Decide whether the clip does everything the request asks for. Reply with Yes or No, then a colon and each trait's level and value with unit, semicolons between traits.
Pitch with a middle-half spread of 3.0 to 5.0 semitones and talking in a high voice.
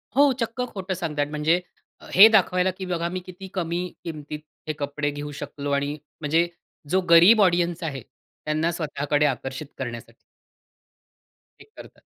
No: average, 3.9 semitones; medium, 165 Hz